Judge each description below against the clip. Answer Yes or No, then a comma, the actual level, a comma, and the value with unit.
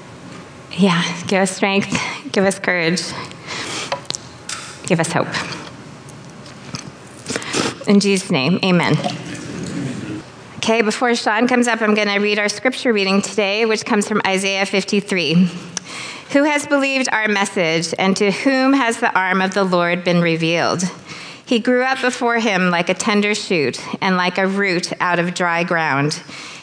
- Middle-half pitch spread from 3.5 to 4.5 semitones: Yes, average, 3.8 semitones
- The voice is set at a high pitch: Yes, high, 195 Hz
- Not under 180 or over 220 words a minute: No, average, 145 wpm